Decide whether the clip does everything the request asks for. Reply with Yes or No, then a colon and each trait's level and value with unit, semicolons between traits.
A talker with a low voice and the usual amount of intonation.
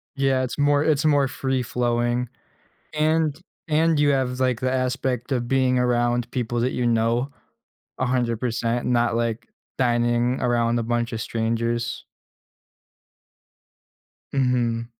No: low, 125 Hz; narrow, 1.9 semitones